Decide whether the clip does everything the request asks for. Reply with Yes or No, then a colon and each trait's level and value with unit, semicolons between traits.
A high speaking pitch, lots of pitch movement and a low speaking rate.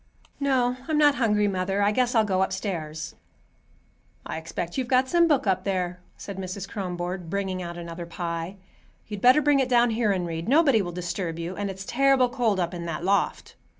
No: high, 195 Hz; wide, 5.7 semitones; average, 190 wpm